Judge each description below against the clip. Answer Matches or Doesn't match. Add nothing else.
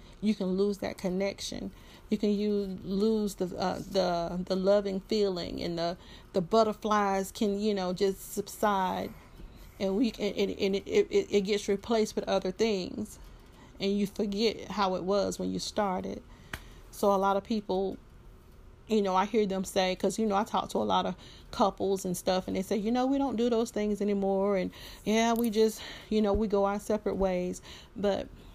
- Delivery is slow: Doesn't match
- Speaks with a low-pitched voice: Doesn't match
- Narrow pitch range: Matches